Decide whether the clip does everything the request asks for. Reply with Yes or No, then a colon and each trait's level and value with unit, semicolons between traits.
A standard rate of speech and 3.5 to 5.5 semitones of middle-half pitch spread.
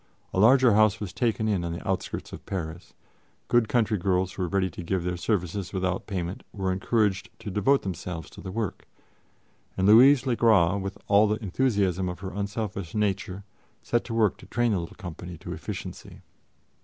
No: average, 185 wpm; average, 3.1 semitones